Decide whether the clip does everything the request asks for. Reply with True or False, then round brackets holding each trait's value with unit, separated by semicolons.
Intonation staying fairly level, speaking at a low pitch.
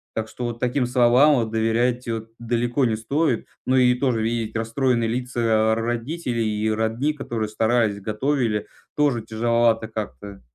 True (2.0 semitones; 115 Hz)